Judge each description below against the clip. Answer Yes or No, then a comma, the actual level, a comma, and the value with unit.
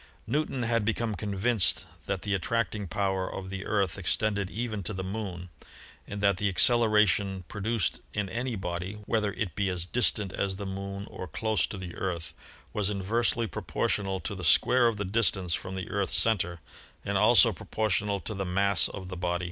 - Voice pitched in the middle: No, low, 100 Hz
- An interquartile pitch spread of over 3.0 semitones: No, narrow, 2.5 semitones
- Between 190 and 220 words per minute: Yes, average, 195 wpm